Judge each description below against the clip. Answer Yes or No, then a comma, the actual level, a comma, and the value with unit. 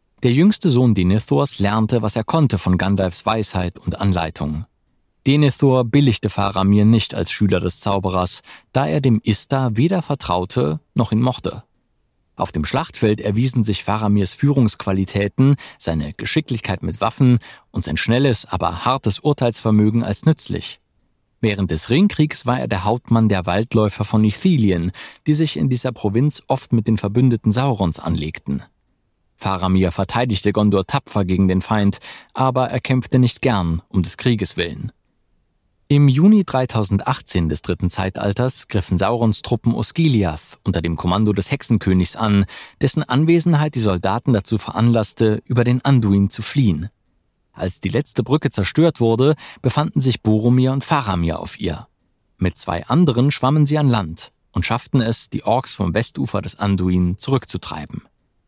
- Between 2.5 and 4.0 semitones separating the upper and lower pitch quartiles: No, average, 5.2 semitones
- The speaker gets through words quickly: No, average, 150 wpm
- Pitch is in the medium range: No, low, 110 Hz